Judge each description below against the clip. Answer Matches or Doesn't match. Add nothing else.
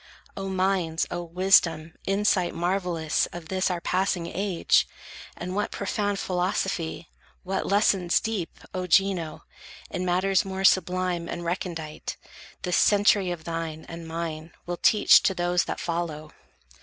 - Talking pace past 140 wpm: Doesn't match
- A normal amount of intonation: Doesn't match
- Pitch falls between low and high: Matches